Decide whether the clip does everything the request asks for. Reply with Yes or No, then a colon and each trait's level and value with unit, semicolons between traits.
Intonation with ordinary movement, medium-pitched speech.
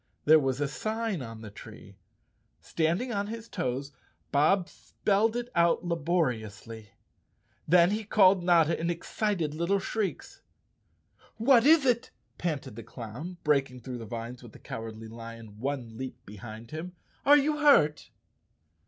No: wide, 9.0 semitones; medium, 155 Hz